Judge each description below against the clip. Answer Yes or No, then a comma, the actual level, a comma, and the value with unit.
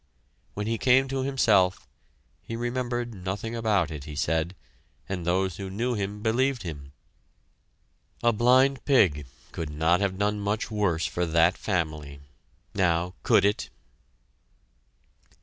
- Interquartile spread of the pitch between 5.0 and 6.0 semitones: Yes, wide, 5.6 semitones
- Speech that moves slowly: Yes, slow, 130 wpm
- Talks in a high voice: No, low, 100 Hz